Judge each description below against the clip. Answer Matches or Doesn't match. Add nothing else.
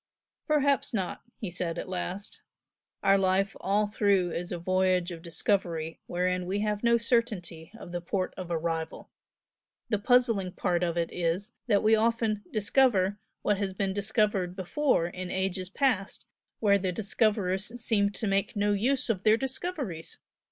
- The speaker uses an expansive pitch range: Doesn't match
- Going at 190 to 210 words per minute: Doesn't match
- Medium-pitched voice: Doesn't match